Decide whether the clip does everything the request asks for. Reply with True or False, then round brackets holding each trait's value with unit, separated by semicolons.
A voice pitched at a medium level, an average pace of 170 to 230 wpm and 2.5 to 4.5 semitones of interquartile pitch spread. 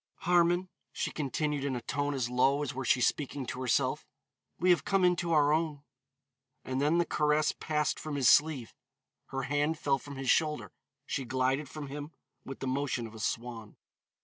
True (145 Hz; 185 wpm; 2.8 semitones)